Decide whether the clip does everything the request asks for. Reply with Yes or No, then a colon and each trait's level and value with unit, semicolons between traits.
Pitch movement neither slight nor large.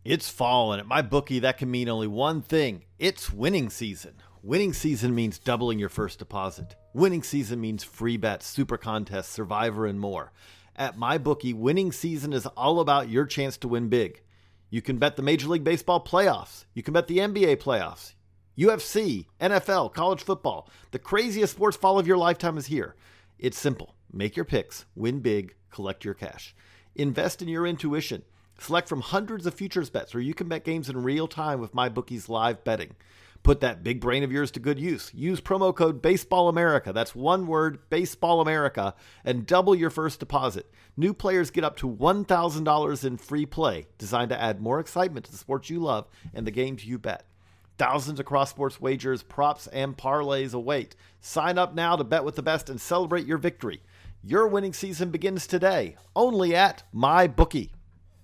No: wide, 7.3 semitones